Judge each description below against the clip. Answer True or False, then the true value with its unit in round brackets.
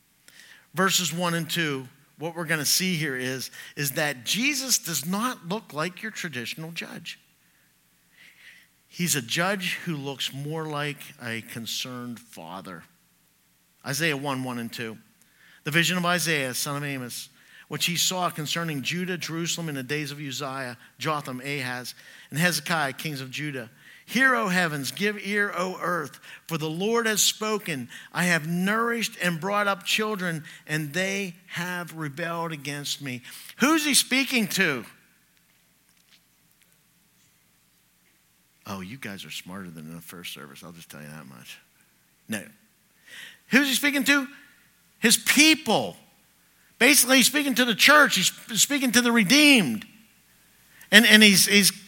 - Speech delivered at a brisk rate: False (150 wpm)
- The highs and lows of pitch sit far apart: True (7.6 semitones)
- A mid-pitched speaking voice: True (165 Hz)